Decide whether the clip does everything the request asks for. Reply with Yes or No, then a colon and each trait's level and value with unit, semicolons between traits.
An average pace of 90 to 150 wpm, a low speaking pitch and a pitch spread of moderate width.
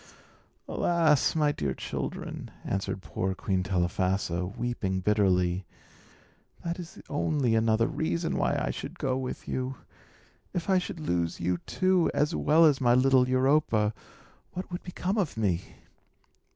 No: average, 140 wpm; low, 125 Hz; wide, 8.8 semitones